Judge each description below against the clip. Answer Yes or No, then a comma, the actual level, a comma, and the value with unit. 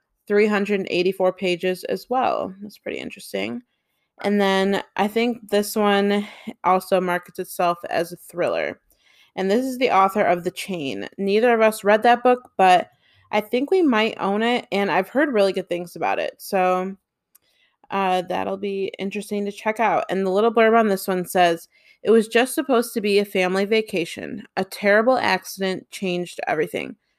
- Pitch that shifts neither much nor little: Yes, average, 3.1 semitones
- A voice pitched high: Yes, high, 200 Hz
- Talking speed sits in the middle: Yes, average, 170 wpm